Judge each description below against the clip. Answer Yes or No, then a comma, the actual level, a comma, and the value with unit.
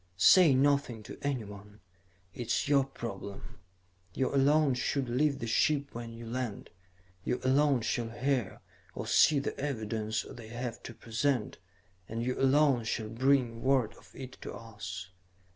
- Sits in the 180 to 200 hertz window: No, low, 125 Hz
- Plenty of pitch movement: No, average, 3.5 semitones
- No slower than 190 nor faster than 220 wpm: No, average, 150 wpm